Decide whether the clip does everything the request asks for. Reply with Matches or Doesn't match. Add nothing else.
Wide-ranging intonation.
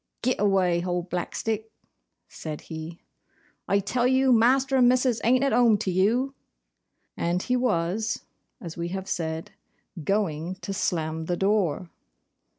Matches